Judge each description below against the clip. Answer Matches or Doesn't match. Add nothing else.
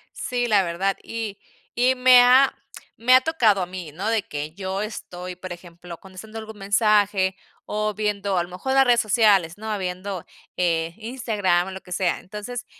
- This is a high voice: Matches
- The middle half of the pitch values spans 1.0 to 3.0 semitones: Doesn't match